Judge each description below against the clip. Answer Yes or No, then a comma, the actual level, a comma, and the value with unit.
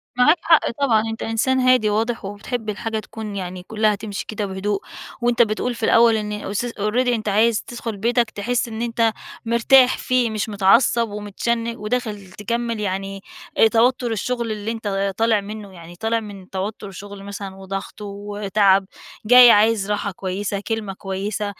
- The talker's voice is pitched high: Yes, high, 215 Hz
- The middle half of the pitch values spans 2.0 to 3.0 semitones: Yes, narrow, 2.5 semitones